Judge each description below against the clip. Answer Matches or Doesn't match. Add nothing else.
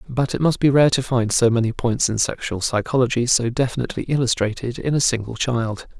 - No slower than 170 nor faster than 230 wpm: Matches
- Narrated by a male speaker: Matches